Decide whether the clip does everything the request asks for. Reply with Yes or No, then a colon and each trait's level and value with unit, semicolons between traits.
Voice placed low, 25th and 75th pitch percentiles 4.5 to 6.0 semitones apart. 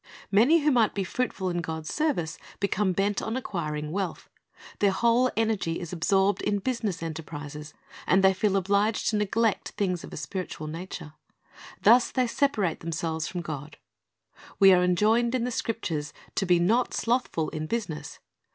No: high, 190 Hz; wide, 5.5 semitones